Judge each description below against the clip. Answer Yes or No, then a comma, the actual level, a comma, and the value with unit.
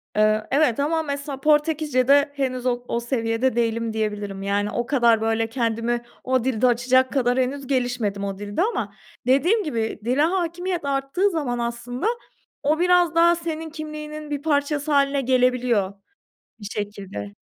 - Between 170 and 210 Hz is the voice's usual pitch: No, very high, 255 Hz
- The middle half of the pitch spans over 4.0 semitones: Yes, average, 4.7 semitones